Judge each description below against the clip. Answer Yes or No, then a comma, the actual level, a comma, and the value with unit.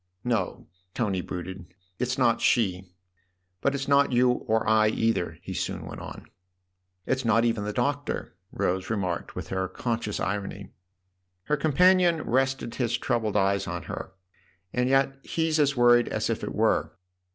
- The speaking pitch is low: Yes, low, 115 Hz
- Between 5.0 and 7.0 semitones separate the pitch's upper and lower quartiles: Yes, average, 5.3 semitones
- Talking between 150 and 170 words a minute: Yes, average, 160 wpm